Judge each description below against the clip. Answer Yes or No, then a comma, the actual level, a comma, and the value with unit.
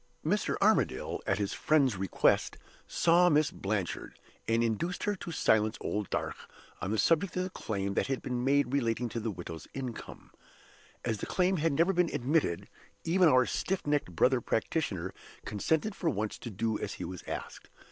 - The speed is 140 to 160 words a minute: No, average, 175 wpm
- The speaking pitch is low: Yes, low, 125 Hz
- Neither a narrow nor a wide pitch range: No, wide, 7.4 semitones